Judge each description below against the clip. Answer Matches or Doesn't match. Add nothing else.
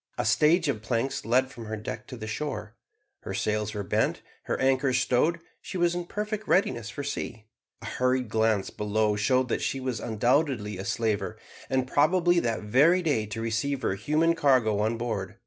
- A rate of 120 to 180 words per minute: Doesn't match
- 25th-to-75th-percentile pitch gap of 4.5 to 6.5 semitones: Matches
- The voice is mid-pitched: Doesn't match